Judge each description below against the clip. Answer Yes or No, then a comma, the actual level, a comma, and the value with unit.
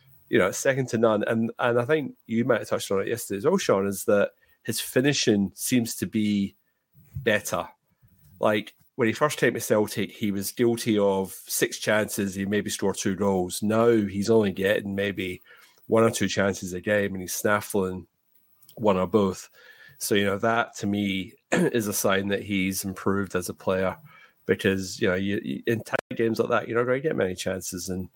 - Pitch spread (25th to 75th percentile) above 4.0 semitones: No, average, 3.0 semitones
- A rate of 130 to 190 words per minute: No, average, 200 wpm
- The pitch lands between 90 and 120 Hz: Yes, low, 100 Hz